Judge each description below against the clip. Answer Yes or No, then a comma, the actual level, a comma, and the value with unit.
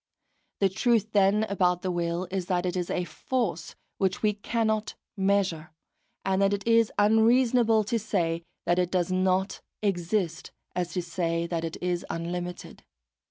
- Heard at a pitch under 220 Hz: Yes, medium, 185 Hz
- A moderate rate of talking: Yes, average, 160 wpm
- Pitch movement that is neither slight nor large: Yes, average, 3.1 semitones